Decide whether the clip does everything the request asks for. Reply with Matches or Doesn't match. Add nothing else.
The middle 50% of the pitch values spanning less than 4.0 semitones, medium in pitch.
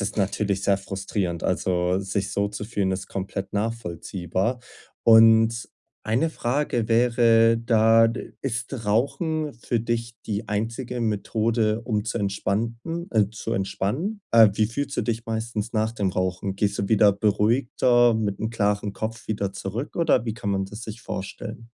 Doesn't match